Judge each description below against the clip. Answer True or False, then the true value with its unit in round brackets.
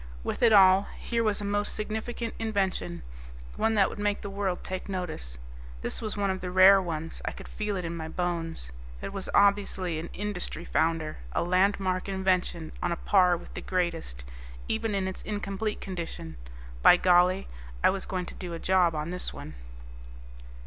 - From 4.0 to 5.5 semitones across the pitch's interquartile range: False (2.8 semitones)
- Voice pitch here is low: False (185 Hz)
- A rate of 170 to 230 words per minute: True (185 wpm)